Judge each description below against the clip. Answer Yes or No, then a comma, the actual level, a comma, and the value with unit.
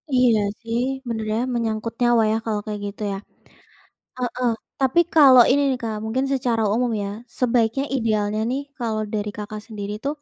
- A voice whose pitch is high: Yes, high, 230 Hz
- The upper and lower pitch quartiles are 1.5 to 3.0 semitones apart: Yes, narrow, 2.6 semitones